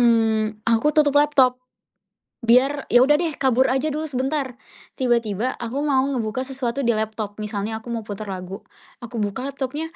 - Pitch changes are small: No, average, 3.7 semitones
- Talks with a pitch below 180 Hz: No, high, 245 Hz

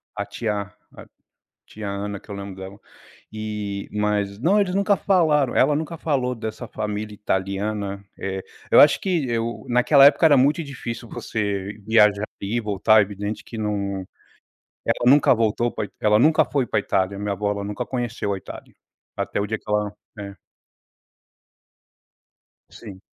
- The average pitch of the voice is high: No, low, 105 Hz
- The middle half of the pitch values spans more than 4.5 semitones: No, average, 3.7 semitones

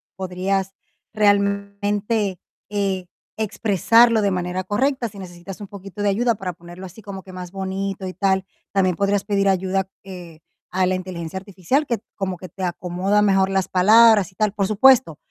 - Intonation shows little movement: Yes, narrow, 1.9 semitones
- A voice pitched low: No, high, 195 Hz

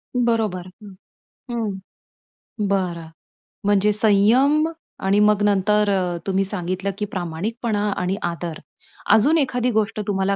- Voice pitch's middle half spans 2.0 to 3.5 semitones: Yes, average, 2.8 semitones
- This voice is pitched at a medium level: No, high, 205 Hz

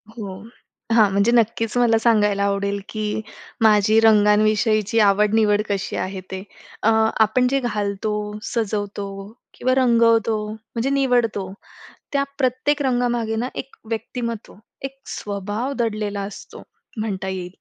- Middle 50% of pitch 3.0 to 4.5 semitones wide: No, narrow, 2.6 semitones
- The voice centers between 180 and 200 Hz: No, high, 220 Hz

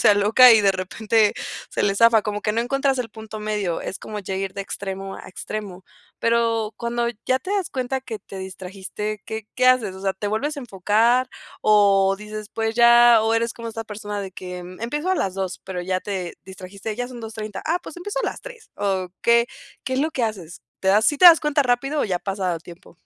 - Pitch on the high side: Yes, high, 215 Hz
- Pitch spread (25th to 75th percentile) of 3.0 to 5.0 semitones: Yes, average, 3.6 semitones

